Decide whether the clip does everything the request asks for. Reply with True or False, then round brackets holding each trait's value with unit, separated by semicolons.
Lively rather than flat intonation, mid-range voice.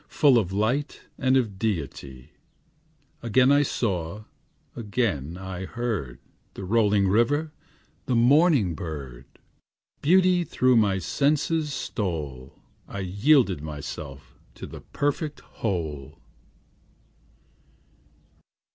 False (8.1 semitones; 105 Hz)